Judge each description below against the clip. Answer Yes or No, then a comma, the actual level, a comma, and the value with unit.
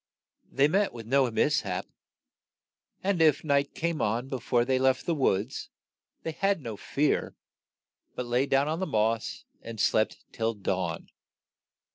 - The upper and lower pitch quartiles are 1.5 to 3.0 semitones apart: No, average, 4.8 semitones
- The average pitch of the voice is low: Yes, low, 130 Hz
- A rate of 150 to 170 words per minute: Yes, average, 155 wpm